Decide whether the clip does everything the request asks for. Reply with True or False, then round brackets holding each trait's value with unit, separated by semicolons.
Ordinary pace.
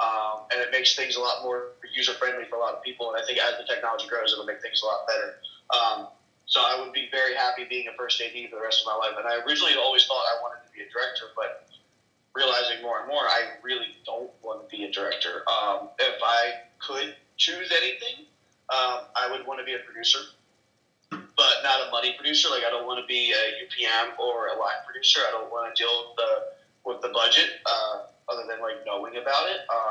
False (235 wpm)